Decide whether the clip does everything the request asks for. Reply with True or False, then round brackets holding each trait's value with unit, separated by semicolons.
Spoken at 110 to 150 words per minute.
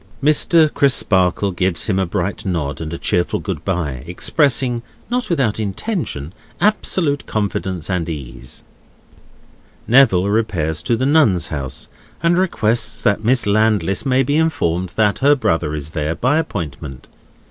True (140 wpm)